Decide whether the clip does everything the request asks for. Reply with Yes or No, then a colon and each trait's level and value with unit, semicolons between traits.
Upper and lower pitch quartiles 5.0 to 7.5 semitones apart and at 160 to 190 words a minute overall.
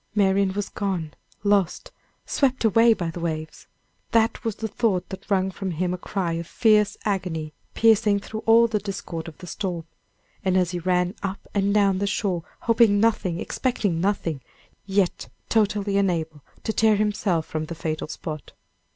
No: average, 3.4 semitones; average, 165 wpm